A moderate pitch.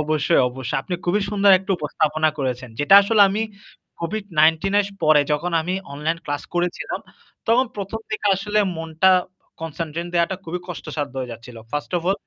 Yes: medium, 165 Hz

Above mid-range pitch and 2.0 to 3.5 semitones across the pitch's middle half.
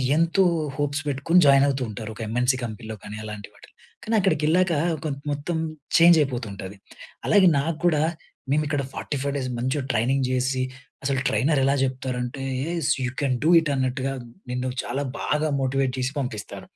No: low, 135 Hz; average, 3.1 semitones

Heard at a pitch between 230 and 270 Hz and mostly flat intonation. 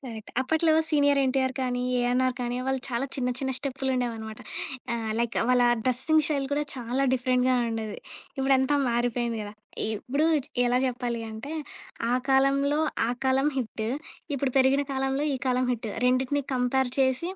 Yes: very high, 260 Hz; narrow, 1.8 semitones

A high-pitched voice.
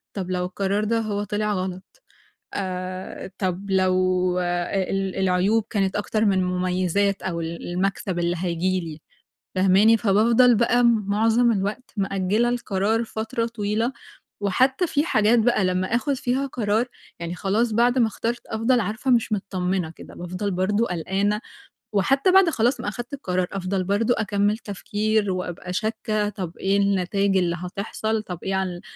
Yes: high, 200 Hz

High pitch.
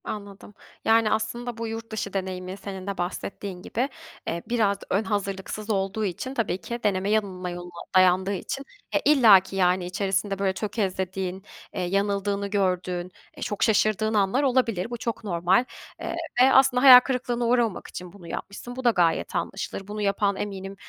Yes: high, 200 Hz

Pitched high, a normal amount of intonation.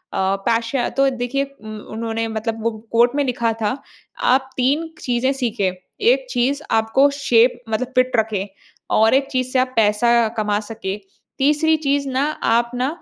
Yes: high, 245 Hz; average, 3.1 semitones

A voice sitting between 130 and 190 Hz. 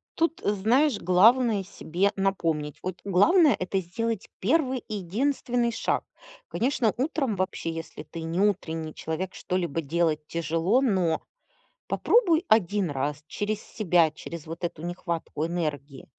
Yes: medium, 185 Hz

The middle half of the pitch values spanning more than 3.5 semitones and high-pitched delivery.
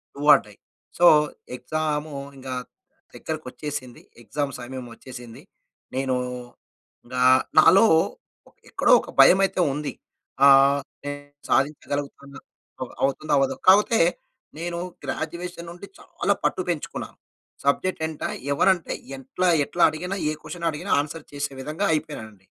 No: average, 4.2 semitones; medium, 150 Hz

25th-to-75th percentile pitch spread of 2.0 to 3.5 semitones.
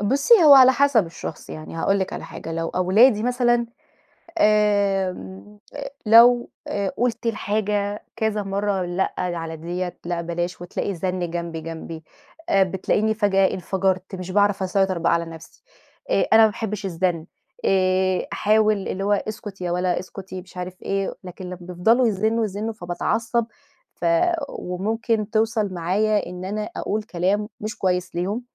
Yes: average, 3.2 semitones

